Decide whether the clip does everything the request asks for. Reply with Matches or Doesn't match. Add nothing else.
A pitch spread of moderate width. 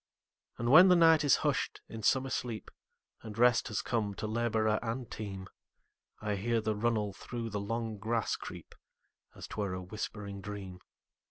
Doesn't match